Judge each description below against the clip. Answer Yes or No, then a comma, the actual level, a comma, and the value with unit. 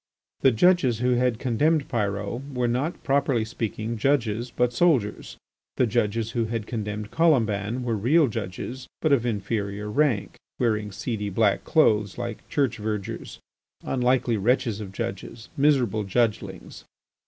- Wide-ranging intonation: No, average, 3.4 semitones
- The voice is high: No, low, 115 Hz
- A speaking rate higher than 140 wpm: No, slow, 135 wpm